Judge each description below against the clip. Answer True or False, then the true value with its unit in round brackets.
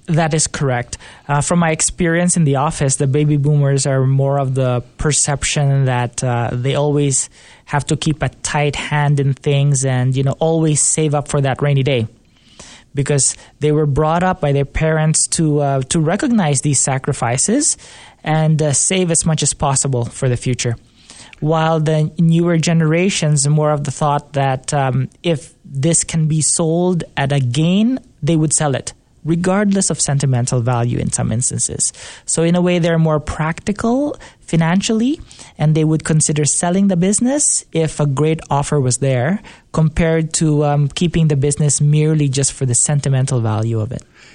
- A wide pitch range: False (3.0 semitones)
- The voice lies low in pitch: False (150 Hz)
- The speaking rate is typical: True (175 wpm)